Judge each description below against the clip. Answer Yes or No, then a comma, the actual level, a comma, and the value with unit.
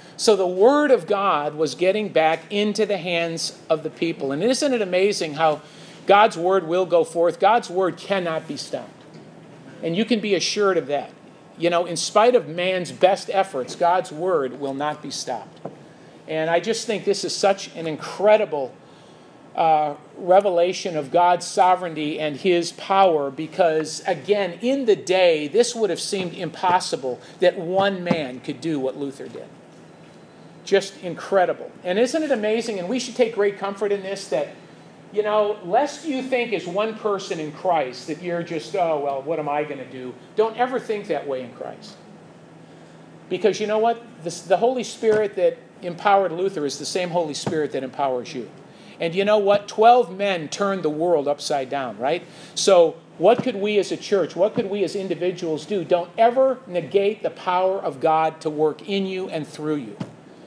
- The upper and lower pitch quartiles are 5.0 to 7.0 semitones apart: No, average, 4.6 semitones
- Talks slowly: No, average, 185 wpm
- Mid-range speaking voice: Yes, medium, 180 Hz